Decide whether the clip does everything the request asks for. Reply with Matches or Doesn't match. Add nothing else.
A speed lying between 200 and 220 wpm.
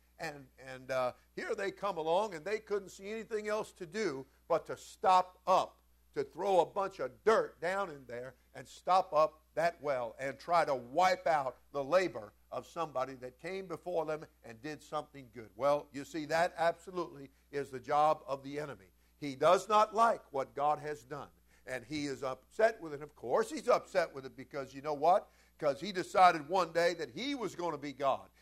Matches